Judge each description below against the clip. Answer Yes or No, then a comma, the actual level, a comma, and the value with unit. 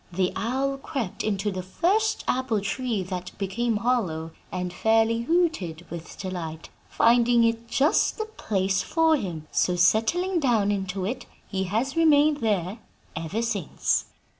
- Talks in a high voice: Yes, high, 220 Hz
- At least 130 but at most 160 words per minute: Yes, average, 140 wpm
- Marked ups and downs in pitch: Yes, wide, 5.8 semitones